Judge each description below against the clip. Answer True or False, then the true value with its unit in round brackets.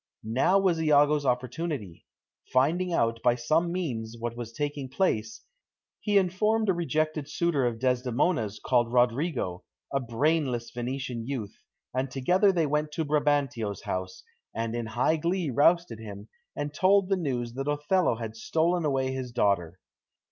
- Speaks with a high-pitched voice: False (135 Hz)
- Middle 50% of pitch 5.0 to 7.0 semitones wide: True (5.6 semitones)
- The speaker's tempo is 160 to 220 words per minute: False (150 wpm)